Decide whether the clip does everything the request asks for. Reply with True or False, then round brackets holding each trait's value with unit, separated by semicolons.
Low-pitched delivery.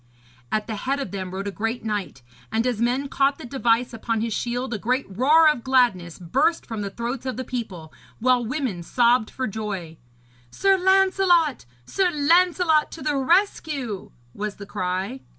False (245 Hz)